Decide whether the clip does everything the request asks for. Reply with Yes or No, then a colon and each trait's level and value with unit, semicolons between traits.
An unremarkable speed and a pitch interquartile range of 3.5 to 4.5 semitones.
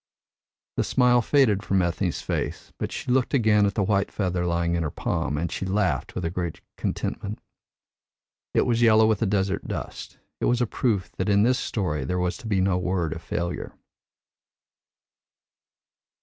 Yes: average, 175 wpm; average, 3.9 semitones